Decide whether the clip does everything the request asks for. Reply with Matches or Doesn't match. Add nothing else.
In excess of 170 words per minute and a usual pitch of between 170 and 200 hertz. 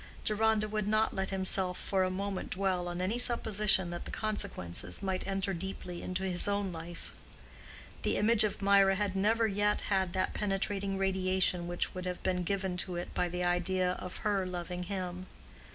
Matches